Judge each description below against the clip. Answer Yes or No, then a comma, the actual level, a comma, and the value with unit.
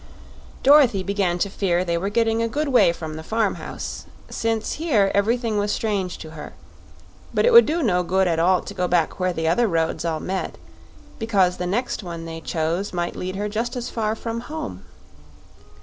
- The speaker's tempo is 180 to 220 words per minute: Yes, average, 195 wpm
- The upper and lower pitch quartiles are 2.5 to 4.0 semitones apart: No, average, 4.7 semitones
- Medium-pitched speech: No, high, 195 Hz